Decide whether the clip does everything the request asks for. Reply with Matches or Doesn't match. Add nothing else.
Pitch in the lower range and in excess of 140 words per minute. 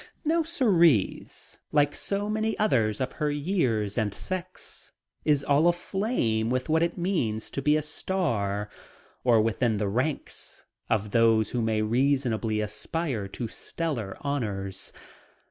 Doesn't match